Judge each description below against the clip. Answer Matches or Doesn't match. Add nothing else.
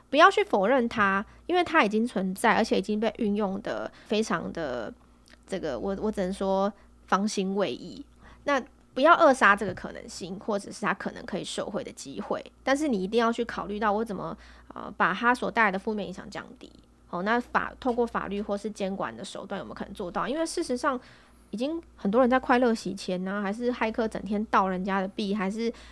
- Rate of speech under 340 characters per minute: Matches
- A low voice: Doesn't match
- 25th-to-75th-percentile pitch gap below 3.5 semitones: Doesn't match